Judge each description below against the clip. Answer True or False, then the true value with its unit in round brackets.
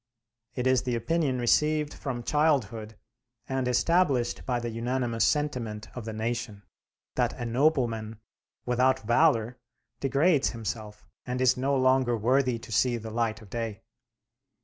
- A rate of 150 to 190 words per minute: False (140 wpm)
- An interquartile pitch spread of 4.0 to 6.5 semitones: False (2.8 semitones)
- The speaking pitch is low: True (120 Hz)